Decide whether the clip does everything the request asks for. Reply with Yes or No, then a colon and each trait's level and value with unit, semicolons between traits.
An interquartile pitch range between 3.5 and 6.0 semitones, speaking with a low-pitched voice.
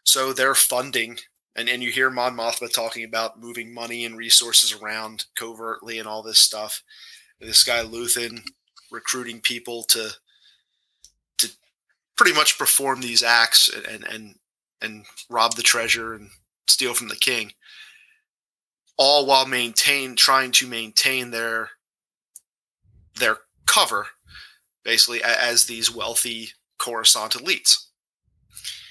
No: narrow, 2.4 semitones; low, 120 Hz